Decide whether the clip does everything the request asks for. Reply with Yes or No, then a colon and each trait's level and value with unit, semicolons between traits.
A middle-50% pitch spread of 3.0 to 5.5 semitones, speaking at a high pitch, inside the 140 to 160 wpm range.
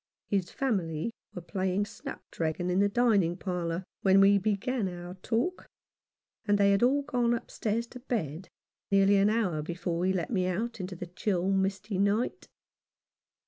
Yes: average, 3.8 semitones; high, 195 Hz; average, 155 wpm